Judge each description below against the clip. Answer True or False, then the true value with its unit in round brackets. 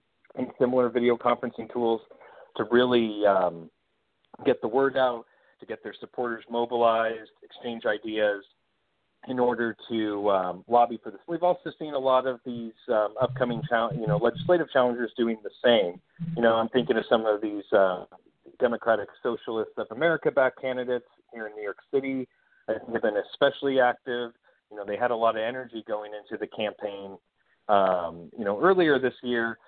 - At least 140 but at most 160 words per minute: False (175 wpm)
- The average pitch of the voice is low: True (120 Hz)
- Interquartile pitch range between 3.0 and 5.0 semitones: False (2.5 semitones)